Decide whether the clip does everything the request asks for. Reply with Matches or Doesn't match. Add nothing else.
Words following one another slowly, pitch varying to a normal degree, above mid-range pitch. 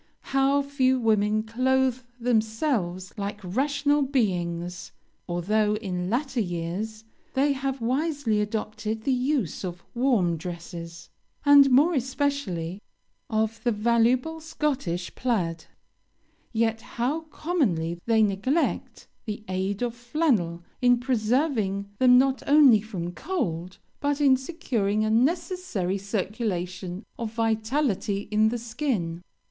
Doesn't match